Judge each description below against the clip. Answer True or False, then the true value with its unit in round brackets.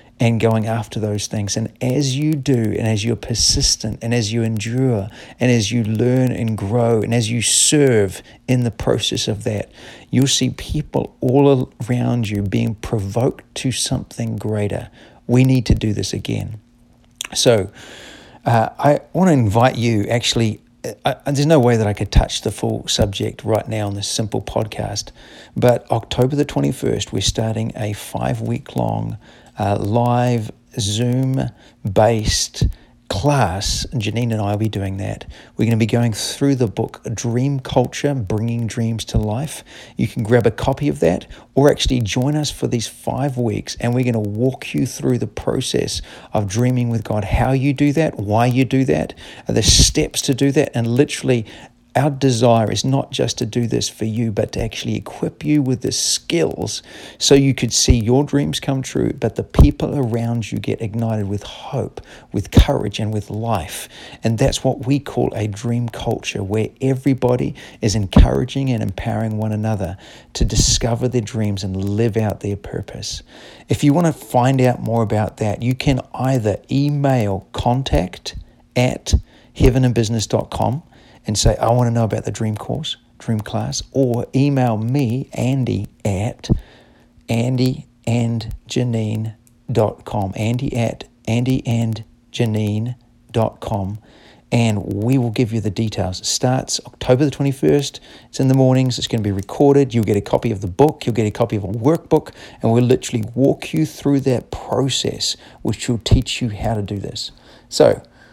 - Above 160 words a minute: True (170 wpm)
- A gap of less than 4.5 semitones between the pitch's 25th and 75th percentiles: True (3.0 semitones)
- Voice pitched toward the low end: True (115 Hz)